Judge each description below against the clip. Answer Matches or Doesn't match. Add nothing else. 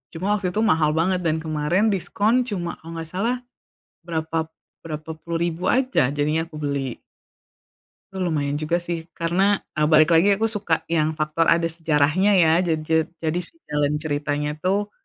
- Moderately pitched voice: Matches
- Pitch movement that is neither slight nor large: Matches